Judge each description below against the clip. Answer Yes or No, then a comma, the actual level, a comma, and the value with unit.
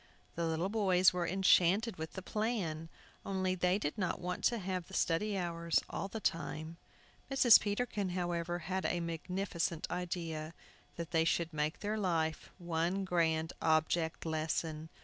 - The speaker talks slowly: No, average, 150 wpm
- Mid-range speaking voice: Yes, medium, 175 Hz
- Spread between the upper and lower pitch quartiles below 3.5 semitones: Yes, average, 2.7 semitones